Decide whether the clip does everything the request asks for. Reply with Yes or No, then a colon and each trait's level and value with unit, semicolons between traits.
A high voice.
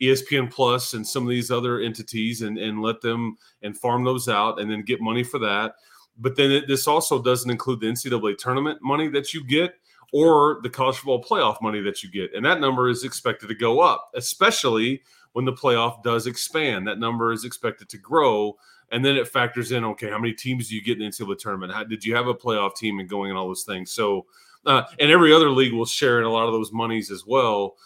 No: low, 120 Hz